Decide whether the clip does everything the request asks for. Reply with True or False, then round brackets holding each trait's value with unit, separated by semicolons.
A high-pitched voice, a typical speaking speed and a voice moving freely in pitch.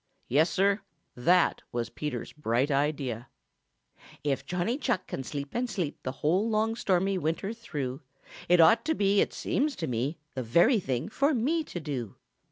False (170 Hz; 175 wpm; 7.7 semitones)